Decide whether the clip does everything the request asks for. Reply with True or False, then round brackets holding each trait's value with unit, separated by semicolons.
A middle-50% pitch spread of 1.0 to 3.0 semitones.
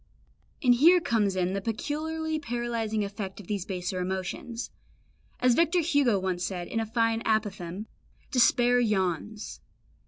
False (4.4 semitones)